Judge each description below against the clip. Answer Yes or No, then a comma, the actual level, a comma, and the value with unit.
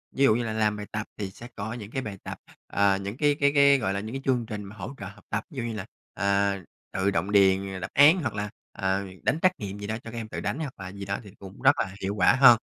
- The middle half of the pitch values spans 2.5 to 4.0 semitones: Yes, average, 3.3 semitones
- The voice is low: Yes, low, 105 Hz